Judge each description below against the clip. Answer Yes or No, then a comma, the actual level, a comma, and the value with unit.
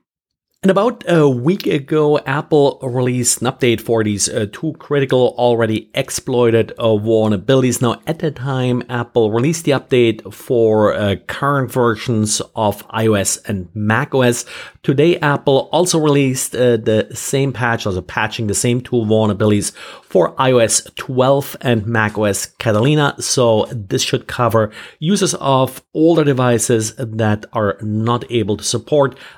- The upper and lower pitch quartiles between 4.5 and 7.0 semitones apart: No, average, 3.9 semitones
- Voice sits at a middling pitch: No, low, 120 Hz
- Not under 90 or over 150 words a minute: Yes, average, 140 wpm